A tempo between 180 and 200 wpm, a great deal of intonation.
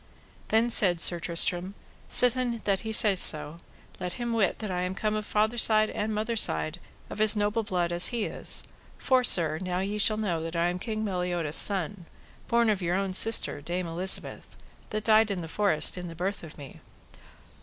No: average, 195 wpm; average, 3.7 semitones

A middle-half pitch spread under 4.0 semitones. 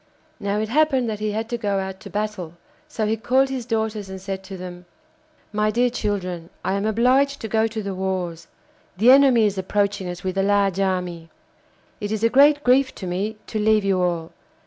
Yes: average, 3.1 semitones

